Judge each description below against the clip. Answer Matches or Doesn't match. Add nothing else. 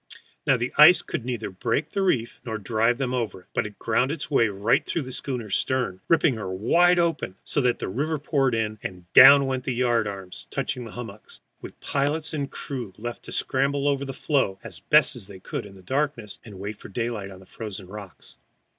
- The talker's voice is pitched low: Matches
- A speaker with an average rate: Doesn't match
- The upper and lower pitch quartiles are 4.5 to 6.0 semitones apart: Matches